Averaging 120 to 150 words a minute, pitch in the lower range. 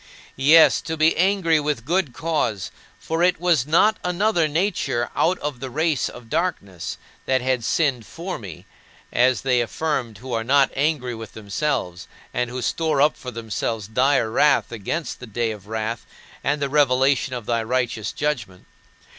No: average, 165 wpm; low, 130 Hz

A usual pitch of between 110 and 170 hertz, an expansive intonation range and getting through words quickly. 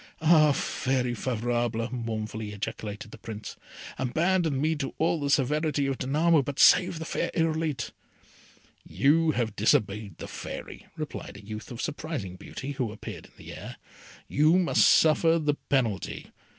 No: low, 135 Hz; wide, 5.9 semitones; average, 150 wpm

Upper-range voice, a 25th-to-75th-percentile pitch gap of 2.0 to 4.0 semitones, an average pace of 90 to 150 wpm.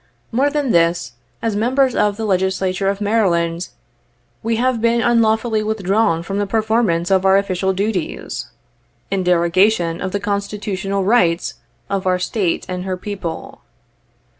Yes: high, 200 Hz; average, 3.3 semitones; average, 145 wpm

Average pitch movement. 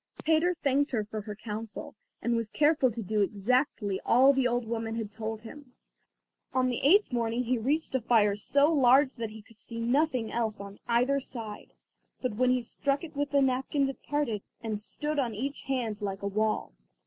Yes: average, 4.1 semitones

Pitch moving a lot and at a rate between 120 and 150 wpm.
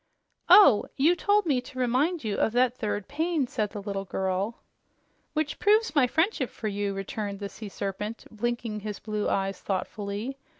No: wide, 5.9 semitones; average, 170 wpm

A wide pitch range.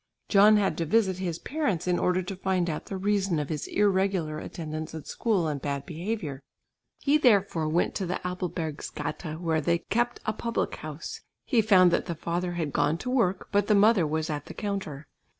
No: average, 4.3 semitones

